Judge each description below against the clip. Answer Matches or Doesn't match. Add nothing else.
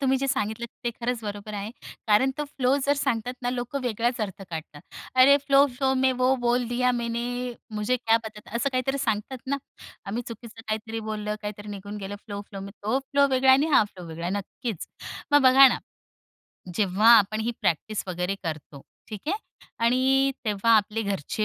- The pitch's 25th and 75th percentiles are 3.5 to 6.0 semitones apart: Matches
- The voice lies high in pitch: Matches